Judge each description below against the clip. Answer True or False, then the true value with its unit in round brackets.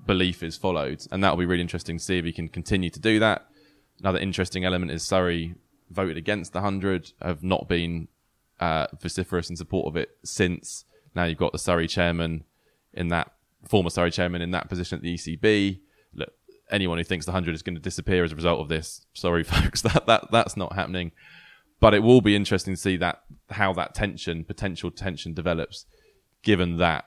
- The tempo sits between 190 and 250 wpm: True (200 wpm)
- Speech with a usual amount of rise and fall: False (2.3 semitones)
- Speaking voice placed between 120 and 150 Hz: False (90 Hz)